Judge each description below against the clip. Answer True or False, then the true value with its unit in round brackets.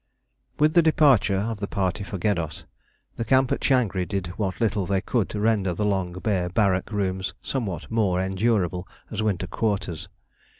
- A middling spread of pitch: True (3.2 semitones)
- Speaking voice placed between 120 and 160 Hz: False (100 Hz)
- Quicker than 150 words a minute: True (170 wpm)